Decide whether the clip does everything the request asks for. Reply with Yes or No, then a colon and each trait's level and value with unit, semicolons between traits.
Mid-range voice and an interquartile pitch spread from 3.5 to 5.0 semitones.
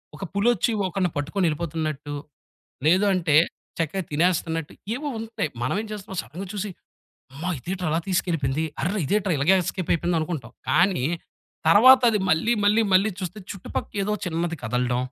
Yes: medium, 175 Hz; average, 4.1 semitones